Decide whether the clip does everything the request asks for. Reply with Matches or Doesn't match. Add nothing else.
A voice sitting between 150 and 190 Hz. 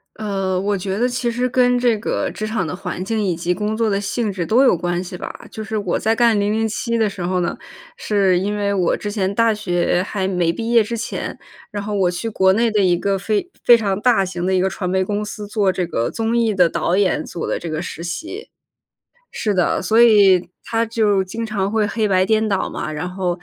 Doesn't match